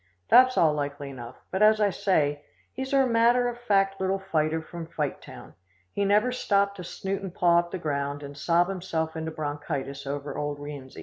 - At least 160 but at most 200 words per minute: Yes, average, 190 wpm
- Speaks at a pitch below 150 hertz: No, medium, 170 Hz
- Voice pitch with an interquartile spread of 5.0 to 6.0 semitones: Yes, wide, 5.4 semitones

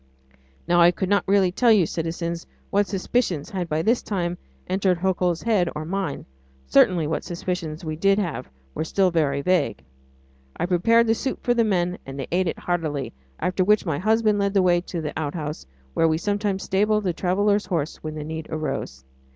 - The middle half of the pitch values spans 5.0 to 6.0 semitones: No, average, 3.8 semitones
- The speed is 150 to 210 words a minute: Yes, average, 190 wpm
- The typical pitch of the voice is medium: Yes, medium, 180 Hz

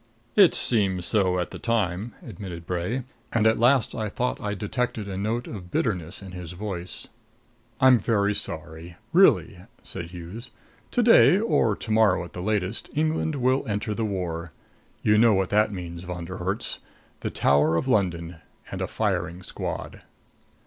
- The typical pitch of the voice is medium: No, low, 100 Hz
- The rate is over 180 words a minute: No, average, 165 wpm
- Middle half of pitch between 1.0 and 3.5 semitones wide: No, average, 4.3 semitones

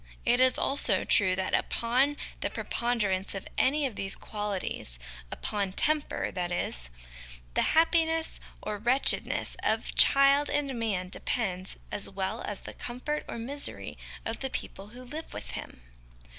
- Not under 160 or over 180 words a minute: No, average, 145 wpm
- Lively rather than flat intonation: Yes, wide, 6.2 semitones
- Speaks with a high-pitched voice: Yes, high, 235 Hz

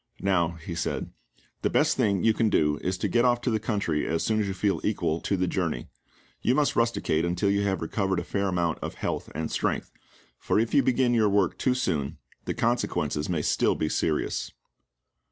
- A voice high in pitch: No, very low, 95 Hz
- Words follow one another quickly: Yes, fast, 210 wpm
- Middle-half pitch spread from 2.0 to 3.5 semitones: No, average, 5.1 semitones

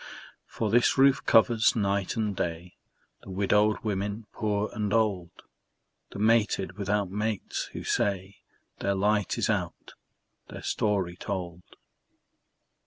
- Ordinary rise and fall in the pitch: No, narrow, 2.1 semitones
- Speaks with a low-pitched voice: Yes, low, 105 Hz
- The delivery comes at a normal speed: No, slow, 120 wpm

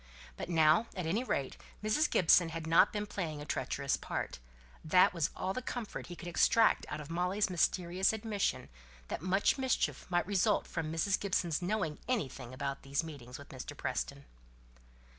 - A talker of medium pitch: Yes, medium, 175 Hz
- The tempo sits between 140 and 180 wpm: Yes, average, 170 wpm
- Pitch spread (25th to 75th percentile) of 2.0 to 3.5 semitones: No, average, 4.7 semitones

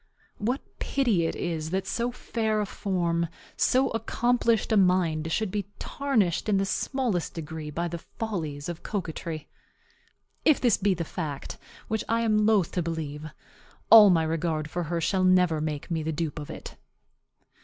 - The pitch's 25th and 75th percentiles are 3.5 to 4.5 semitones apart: No, average, 5.1 semitones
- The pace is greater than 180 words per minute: No, average, 165 wpm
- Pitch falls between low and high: Yes, medium, 180 Hz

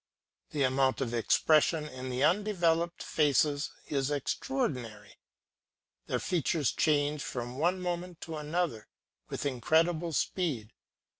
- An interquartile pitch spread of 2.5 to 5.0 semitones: Yes, average, 4.6 semitones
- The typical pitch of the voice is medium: Yes, medium, 150 Hz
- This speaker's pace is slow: Yes, slow, 115 wpm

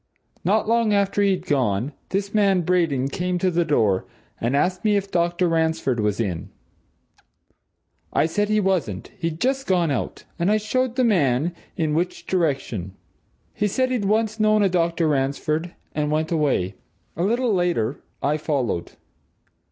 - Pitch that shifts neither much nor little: No, wide, 6.0 semitones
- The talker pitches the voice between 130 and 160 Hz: No, medium, 170 Hz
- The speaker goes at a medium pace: Yes, average, 160 wpm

